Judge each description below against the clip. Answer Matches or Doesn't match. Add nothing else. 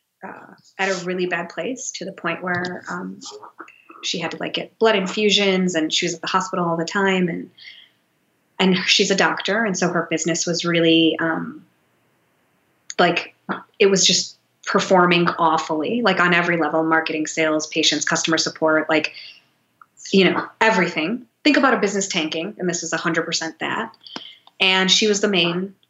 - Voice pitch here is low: Doesn't match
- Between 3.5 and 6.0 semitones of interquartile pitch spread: Doesn't match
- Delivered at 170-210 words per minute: Matches